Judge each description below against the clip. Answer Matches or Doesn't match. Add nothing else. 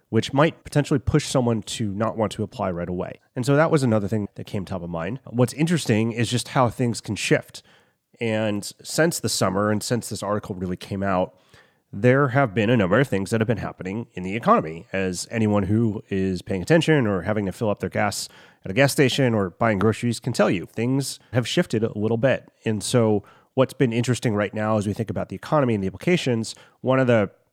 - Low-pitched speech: Matches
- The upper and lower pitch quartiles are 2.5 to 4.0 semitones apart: Matches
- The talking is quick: Matches